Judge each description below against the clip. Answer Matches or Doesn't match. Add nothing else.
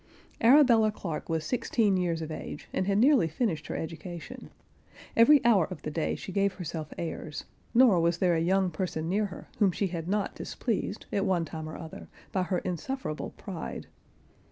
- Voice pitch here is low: Doesn't match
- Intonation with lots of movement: Doesn't match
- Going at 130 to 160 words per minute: Doesn't match